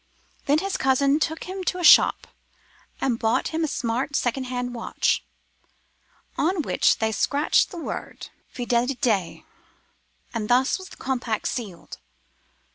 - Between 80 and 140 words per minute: Yes, slow, 135 wpm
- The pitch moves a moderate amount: Yes, average, 4.7 semitones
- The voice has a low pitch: No, very high, 260 Hz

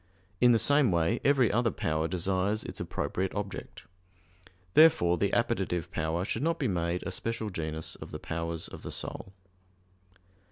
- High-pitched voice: No, very low, 95 Hz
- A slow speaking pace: No, average, 160 wpm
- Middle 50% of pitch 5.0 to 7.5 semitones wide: Yes, wide, 5.6 semitones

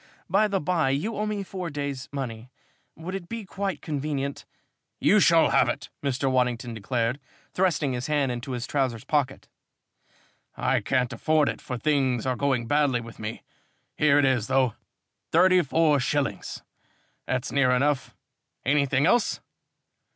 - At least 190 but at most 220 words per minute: No, average, 155 wpm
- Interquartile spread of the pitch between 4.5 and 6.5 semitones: No, average, 3.6 semitones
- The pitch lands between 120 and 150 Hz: Yes, medium, 140 Hz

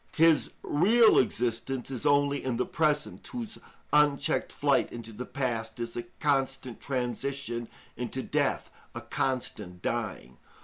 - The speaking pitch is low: Yes, low, 130 Hz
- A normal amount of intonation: Yes, average, 3.5 semitones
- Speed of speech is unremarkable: No, slow, 130 wpm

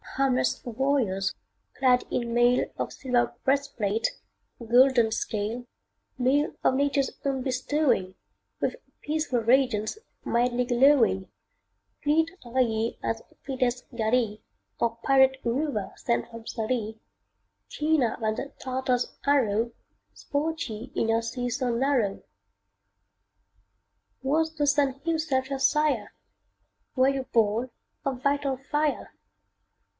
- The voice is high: Yes, very high, 255 Hz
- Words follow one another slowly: Yes, slow, 110 wpm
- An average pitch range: Yes, average, 3.2 semitones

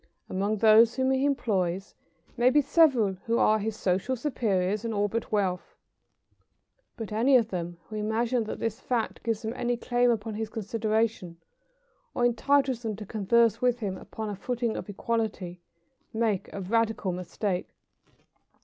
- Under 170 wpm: Yes, average, 160 wpm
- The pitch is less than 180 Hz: No, high, 220 Hz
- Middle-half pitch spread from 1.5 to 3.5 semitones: Yes, average, 2.8 semitones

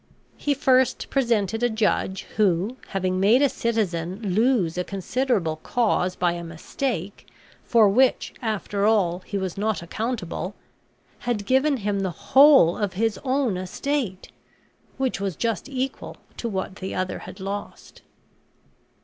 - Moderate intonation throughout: Yes, average, 4.7 semitones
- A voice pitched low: No, high, 205 Hz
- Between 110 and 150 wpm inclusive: Yes, average, 140 wpm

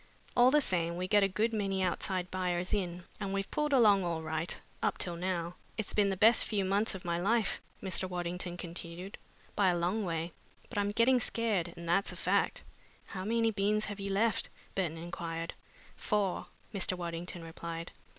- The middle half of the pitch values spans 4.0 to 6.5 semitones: No, average, 3.1 semitones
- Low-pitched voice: No, medium, 185 Hz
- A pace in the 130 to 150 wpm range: No, average, 185 wpm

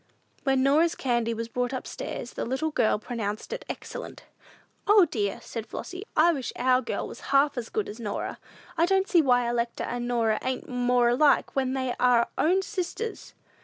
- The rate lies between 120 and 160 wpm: No, average, 185 wpm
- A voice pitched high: Yes, very high, 255 Hz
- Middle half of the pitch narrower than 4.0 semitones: No, average, 4.8 semitones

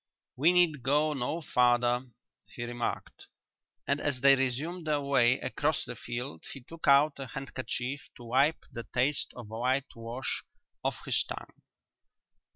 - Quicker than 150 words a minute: No, average, 145 wpm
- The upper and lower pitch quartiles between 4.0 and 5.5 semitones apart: No, average, 3.2 semitones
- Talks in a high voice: No, low, 130 Hz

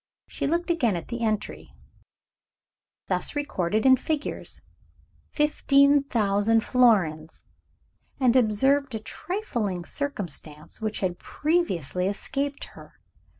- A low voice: No, high, 235 Hz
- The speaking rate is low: Yes, slow, 100 wpm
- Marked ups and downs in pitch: Yes, wide, 6.2 semitones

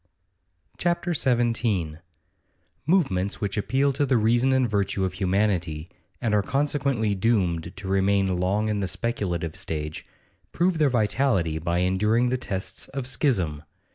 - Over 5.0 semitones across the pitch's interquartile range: Yes, wide, 5.6 semitones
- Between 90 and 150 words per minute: Yes, average, 140 wpm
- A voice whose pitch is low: Yes, low, 105 Hz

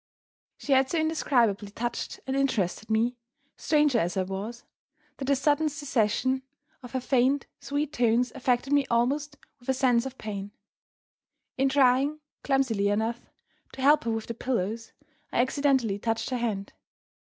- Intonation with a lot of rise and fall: No, average, 3.5 semitones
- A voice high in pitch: Yes, very high, 250 Hz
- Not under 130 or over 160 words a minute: Yes, average, 150 wpm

